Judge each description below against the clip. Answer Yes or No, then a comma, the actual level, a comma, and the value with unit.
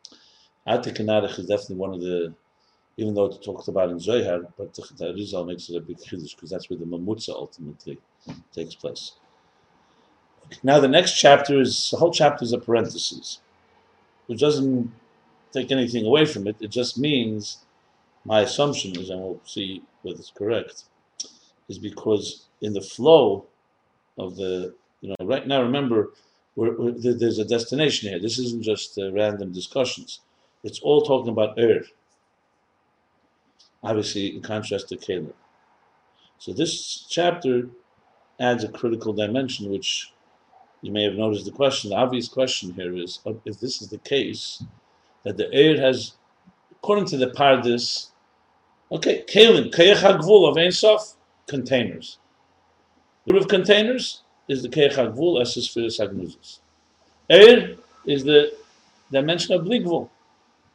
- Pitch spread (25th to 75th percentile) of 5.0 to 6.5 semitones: Yes, wide, 5.6 semitones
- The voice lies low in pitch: Yes, low, 120 Hz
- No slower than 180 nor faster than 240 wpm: No, average, 150 wpm